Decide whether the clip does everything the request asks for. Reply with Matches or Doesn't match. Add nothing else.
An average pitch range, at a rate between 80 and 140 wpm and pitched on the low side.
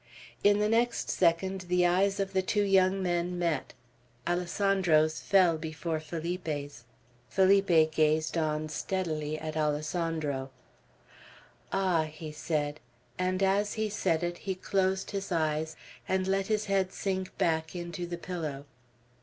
Doesn't match